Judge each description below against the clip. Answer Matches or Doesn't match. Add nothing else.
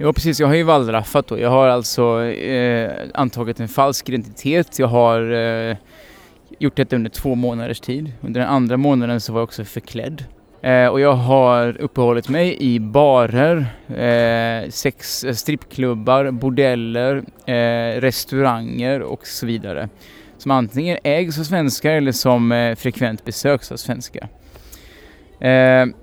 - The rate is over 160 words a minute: Doesn't match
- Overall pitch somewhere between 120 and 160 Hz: Matches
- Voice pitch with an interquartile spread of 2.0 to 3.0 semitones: Matches